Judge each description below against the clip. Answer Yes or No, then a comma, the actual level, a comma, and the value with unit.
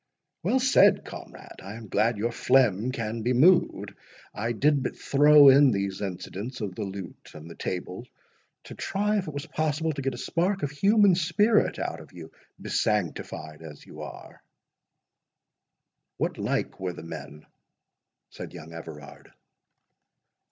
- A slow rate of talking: No, average, 150 wpm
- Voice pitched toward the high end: No, low, 120 Hz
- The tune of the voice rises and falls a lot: Yes, wide, 8.0 semitones